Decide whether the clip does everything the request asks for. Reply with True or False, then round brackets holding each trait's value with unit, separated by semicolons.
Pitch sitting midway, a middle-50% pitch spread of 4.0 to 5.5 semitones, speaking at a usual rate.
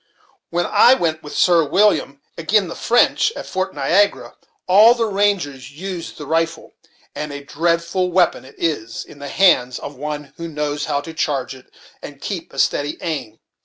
True (160 Hz; 4.3 semitones; 175 wpm)